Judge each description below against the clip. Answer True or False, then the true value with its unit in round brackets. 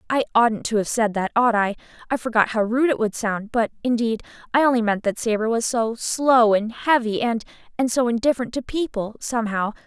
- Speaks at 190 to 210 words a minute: True (200 wpm)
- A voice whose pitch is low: False (230 Hz)